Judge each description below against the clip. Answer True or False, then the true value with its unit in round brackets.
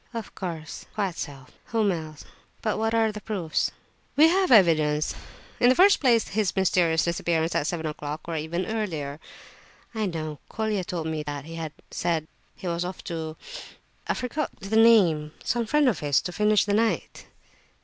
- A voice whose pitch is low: False (180 Hz)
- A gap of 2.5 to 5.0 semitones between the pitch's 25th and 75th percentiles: False (5.6 semitones)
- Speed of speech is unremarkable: True (170 wpm)